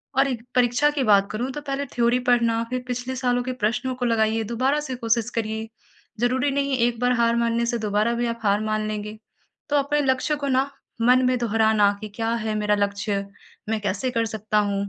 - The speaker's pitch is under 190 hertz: No, high, 235 Hz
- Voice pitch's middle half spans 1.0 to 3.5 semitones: Yes, average, 2.8 semitones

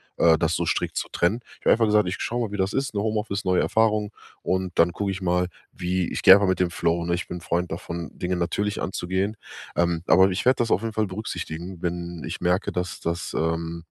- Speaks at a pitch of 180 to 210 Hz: No, very low, 90 Hz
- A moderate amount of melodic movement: Yes, average, 3.1 semitones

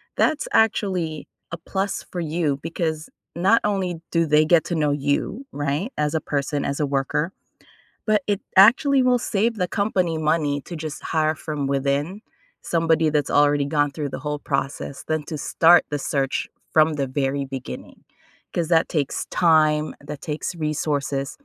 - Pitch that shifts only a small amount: No, average, 3.3 semitones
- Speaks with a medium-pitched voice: Yes, medium, 155 Hz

